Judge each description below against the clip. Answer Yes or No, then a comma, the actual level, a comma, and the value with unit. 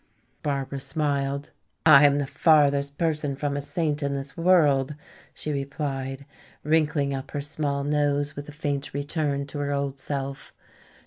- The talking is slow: No, average, 150 wpm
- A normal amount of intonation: No, narrow, 1.1 semitones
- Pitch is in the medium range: Yes, medium, 145 Hz